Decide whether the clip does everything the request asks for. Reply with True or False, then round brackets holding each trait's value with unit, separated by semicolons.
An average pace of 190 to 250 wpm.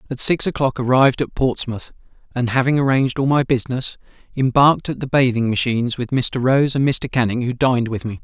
True (195 wpm)